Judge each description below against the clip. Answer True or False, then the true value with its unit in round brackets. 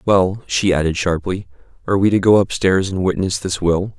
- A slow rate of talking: False (195 wpm)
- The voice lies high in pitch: False (95 Hz)